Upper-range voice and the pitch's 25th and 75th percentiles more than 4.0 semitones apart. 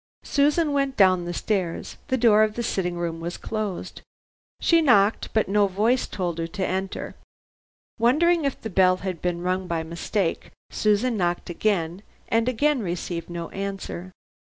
Yes: high, 195 Hz; average, 4.7 semitones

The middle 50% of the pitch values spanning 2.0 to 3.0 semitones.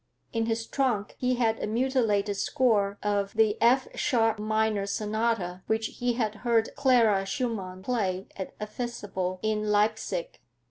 Yes: narrow, 2.5 semitones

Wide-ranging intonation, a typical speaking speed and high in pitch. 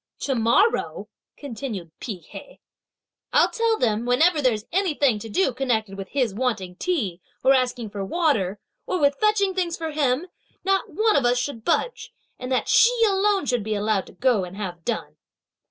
Yes: wide, 8.7 semitones; average, 180 wpm; very high, 255 Hz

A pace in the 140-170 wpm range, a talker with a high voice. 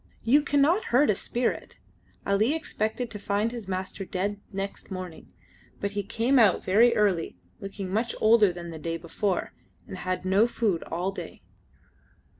Yes: average, 160 wpm; high, 205 Hz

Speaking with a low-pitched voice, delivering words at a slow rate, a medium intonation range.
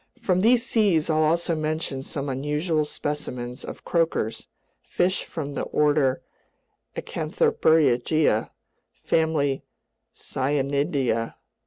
No: medium, 150 Hz; slow, 95 wpm; average, 3.2 semitones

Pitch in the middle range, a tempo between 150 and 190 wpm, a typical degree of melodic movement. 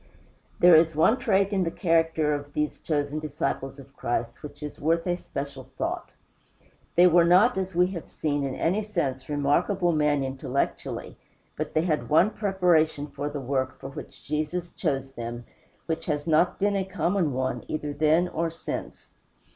Yes: medium, 155 Hz; average, 170 wpm; average, 3.6 semitones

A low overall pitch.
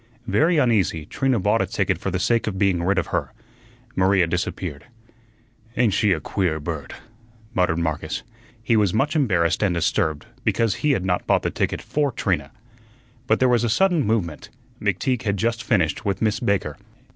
Yes: low, 100 Hz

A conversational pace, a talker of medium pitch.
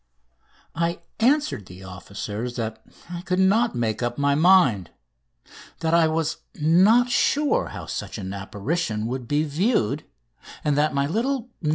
Yes: average, 150 wpm; medium, 150 Hz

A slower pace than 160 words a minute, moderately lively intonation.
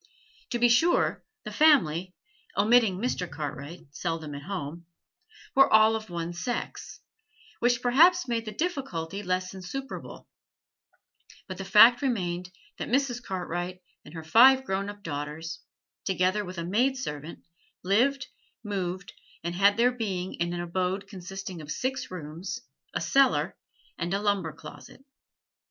No: average, 140 wpm; wide, 5.7 semitones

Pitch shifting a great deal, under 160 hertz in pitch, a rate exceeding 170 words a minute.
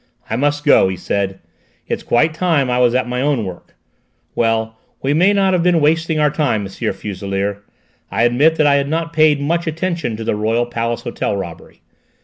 Yes: wide, 6.1 semitones; low, 135 Hz; average, 190 wpm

